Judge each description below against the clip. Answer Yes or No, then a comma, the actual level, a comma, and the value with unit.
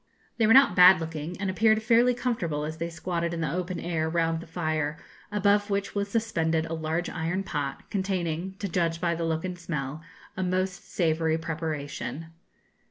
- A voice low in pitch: No, medium, 170 Hz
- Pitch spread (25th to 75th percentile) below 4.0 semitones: Yes, average, 3.0 semitones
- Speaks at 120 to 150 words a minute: No, average, 180 wpm